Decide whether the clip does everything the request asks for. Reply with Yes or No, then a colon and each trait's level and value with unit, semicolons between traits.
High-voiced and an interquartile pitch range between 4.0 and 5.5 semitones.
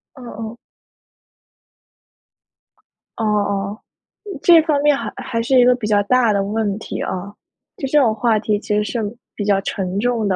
No: high, 220 Hz; average, 3.3 semitones